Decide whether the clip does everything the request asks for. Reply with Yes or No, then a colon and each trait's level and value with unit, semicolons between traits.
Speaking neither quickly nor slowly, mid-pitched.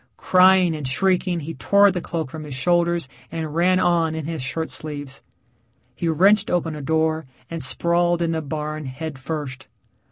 Yes: average, 170 wpm; medium, 160 Hz